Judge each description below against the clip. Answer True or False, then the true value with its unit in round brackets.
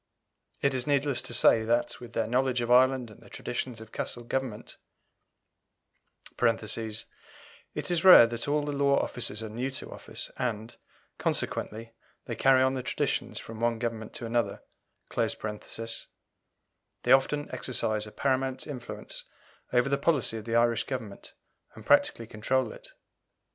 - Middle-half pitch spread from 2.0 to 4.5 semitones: True (2.8 semitones)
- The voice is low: True (120 Hz)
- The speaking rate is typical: True (150 wpm)